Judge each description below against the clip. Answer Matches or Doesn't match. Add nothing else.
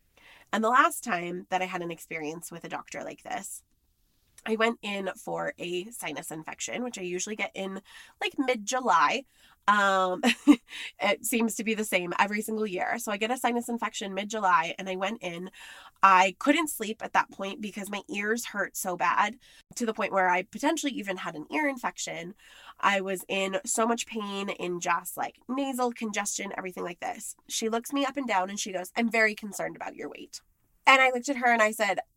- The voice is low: Doesn't match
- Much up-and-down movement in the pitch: Doesn't match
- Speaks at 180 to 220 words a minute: Matches